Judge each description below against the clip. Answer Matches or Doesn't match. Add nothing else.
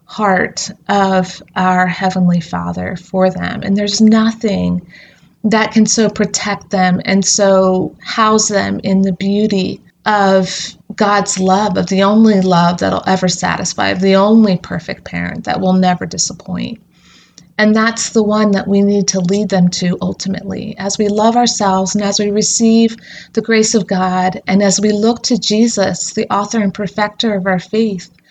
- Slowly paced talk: Doesn't match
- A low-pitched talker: Doesn't match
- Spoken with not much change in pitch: Matches